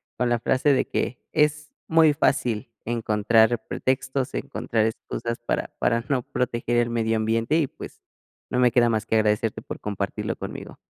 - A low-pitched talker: Yes, low, 120 Hz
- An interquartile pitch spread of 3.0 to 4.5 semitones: No, narrow, 2.6 semitones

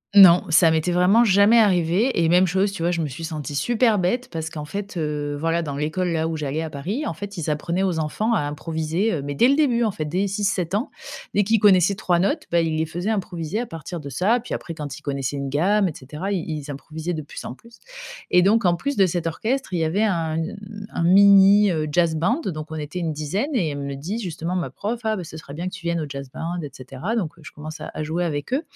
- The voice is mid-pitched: Yes, medium, 170 Hz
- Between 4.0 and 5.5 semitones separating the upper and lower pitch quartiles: Yes, average, 4.5 semitones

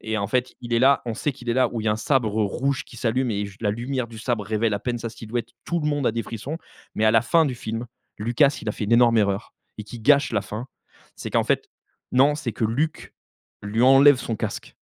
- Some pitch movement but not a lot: Yes, average, 3.1 semitones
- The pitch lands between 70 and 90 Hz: No, low, 115 Hz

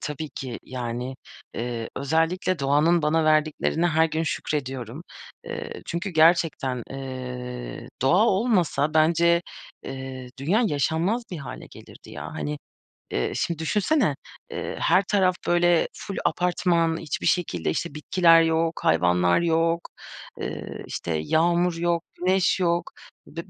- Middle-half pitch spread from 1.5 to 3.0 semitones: No, average, 4.6 semitones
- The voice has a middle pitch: Yes, medium, 160 Hz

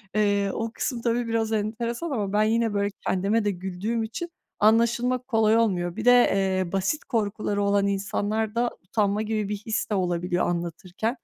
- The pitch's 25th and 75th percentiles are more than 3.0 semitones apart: No, narrow, 2.5 semitones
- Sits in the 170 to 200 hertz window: No, high, 215 Hz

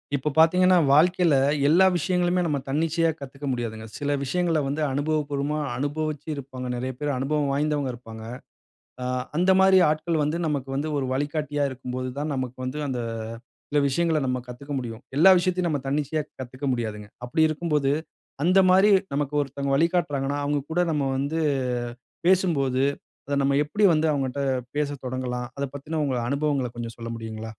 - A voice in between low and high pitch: Yes, medium, 145 Hz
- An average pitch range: Yes, average, 3.3 semitones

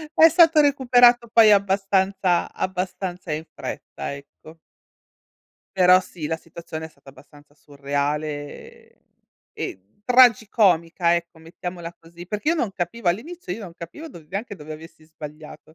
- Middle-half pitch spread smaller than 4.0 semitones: No, average, 5.1 semitones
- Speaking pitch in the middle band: Yes, medium, 175 Hz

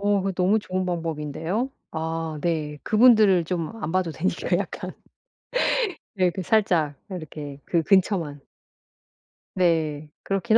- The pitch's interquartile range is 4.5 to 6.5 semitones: No, average, 3.6 semitones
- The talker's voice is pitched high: No, medium, 175 Hz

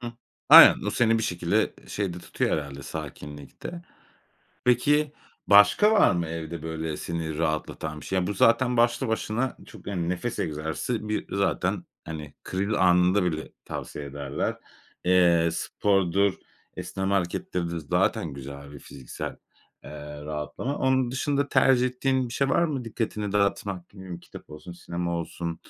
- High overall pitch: No, very low, 90 Hz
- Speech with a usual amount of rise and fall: No, wide, 6.5 semitones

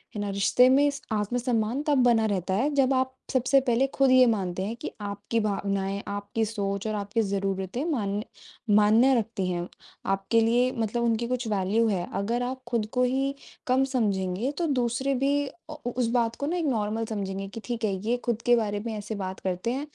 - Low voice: No, high, 225 Hz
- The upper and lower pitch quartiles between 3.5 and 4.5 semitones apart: Yes, average, 3.9 semitones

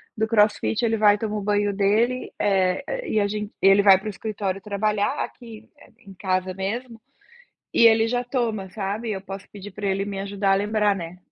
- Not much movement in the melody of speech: Yes, narrow, 2.2 semitones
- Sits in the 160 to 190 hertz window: No, high, 205 Hz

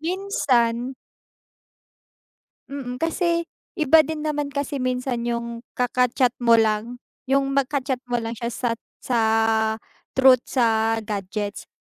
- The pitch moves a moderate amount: Yes, average, 3.2 semitones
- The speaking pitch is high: Yes, very high, 250 Hz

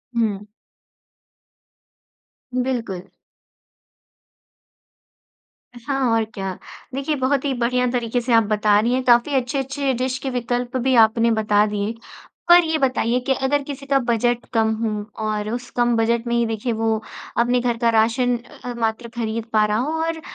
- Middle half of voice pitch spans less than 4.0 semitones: Yes, narrow, 2.6 semitones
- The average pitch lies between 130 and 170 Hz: No, high, 240 Hz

